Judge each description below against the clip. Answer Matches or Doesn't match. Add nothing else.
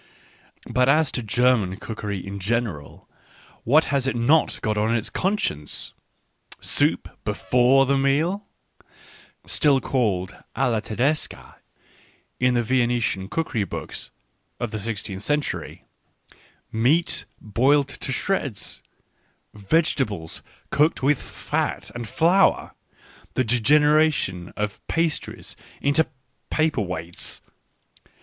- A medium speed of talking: Doesn't match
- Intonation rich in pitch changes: Matches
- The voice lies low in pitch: Matches